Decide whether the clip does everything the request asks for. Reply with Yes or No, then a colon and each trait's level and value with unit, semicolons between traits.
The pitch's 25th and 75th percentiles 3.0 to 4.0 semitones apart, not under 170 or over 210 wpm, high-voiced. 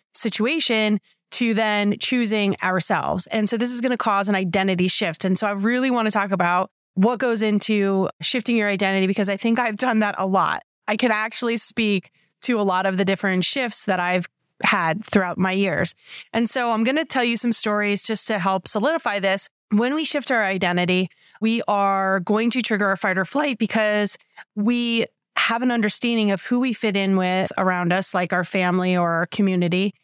Yes: average, 3.3 semitones; average, 200 wpm; high, 210 Hz